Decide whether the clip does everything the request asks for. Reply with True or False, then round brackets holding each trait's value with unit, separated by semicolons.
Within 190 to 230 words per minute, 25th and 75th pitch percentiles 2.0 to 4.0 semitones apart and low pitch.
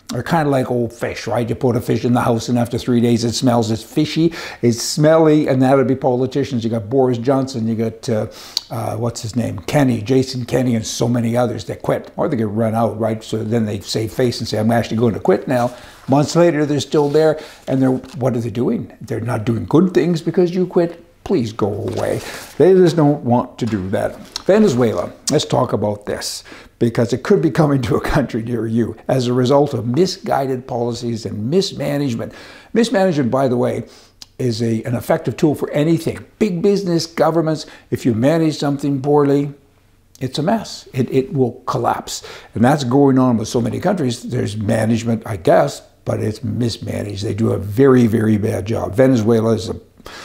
True (205 wpm; 3.6 semitones; 125 Hz)